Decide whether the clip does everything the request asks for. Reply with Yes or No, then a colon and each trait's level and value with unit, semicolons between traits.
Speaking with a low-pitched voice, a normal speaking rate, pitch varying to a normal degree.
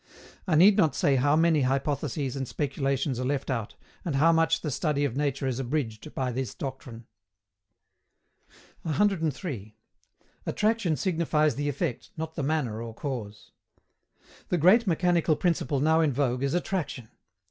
No: medium, 145 Hz; average, 145 wpm; average, 3.8 semitones